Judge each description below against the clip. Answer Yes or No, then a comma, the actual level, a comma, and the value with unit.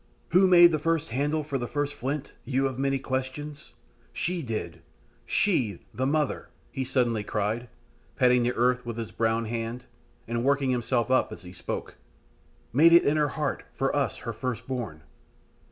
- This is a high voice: No, low, 130 Hz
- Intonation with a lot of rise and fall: No, average, 3.8 semitones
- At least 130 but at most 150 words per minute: No, average, 175 wpm